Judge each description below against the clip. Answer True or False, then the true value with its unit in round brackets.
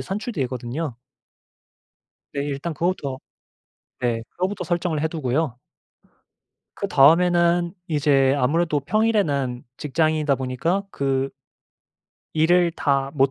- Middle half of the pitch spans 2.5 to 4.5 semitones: True (4.2 semitones)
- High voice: False (150 Hz)